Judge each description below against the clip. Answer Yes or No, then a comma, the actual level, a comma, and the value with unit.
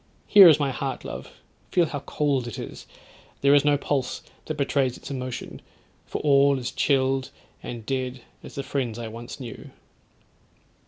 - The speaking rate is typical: Yes, average, 165 wpm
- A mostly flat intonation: Yes, narrow, 2.2 semitones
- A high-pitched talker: No, low, 135 Hz